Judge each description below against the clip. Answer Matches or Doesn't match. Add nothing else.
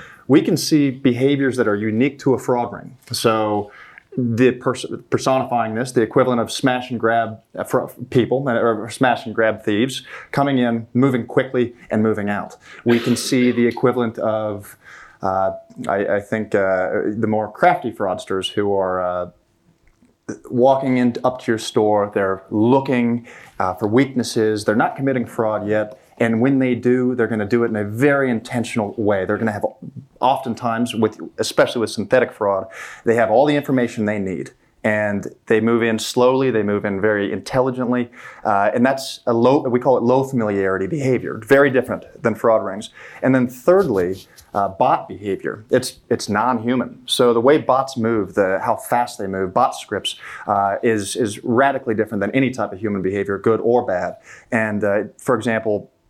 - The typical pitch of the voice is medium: Doesn't match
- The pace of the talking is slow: Doesn't match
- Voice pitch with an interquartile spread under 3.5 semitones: Matches